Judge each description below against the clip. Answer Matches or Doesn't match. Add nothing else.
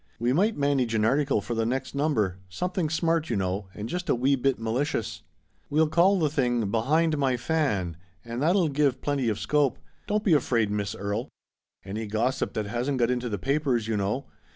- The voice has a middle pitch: Doesn't match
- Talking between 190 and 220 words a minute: Matches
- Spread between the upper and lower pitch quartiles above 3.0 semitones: Matches